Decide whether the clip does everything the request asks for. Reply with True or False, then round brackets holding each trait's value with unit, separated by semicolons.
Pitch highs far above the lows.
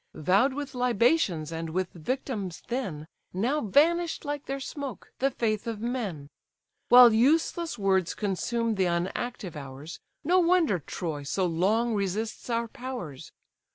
True (6.4 semitones)